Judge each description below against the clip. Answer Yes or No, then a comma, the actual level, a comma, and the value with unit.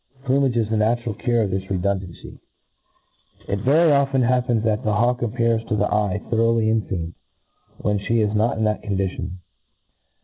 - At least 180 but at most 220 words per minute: No, average, 165 wpm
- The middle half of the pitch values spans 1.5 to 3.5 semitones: Yes, average, 2.9 semitones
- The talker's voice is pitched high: No, low, 110 Hz